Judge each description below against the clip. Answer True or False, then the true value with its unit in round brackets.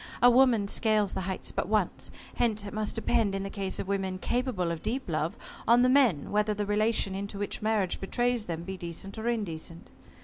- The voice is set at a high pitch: True (205 Hz)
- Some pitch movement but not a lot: True (3.2 semitones)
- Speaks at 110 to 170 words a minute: False (205 wpm)